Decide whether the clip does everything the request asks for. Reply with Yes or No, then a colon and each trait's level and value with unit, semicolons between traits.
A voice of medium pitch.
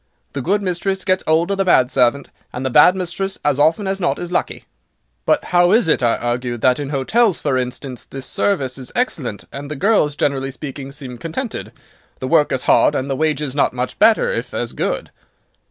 Yes: medium, 145 Hz